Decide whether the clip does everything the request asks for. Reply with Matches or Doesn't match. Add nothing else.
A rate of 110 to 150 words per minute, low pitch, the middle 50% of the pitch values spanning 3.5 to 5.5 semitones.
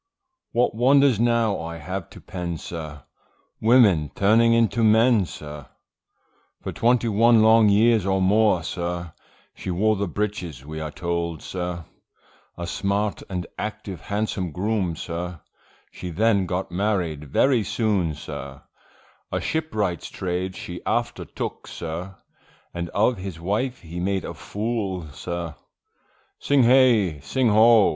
Matches